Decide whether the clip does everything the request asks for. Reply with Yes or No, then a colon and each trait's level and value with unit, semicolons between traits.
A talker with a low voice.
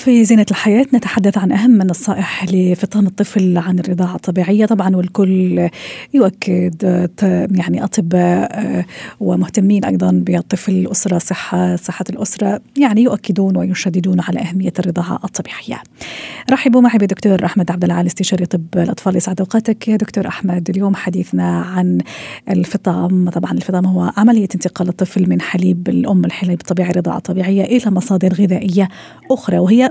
No: medium, 185 Hz